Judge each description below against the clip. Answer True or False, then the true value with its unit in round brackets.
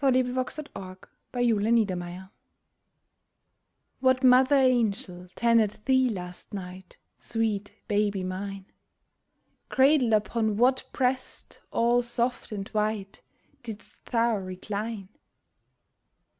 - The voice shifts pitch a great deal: False (4.0 semitones)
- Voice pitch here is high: True (225 Hz)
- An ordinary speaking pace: False (90 wpm)